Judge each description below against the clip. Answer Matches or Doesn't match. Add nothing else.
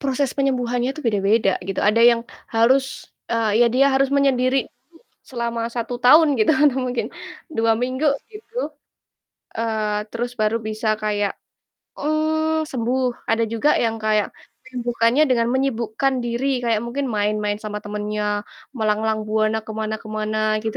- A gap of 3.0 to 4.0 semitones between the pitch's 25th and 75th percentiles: Matches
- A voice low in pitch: Doesn't match